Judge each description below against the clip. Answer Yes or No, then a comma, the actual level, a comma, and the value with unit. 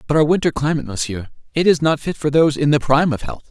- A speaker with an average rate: No, fast, 255 wpm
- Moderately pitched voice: Yes, medium, 145 Hz